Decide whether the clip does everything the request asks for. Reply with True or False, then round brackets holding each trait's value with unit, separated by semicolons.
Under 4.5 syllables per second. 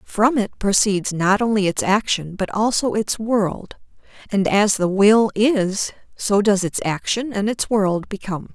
True (4.1 syllables/s)